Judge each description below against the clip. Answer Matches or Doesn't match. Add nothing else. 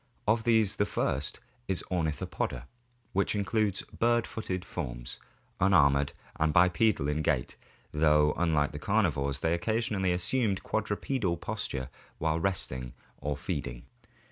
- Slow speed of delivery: Matches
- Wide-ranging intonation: Matches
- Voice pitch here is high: Doesn't match